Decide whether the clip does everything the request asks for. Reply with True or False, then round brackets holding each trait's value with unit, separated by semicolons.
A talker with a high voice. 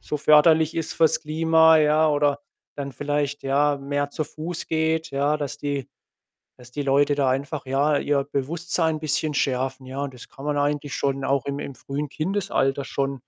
False (145 Hz)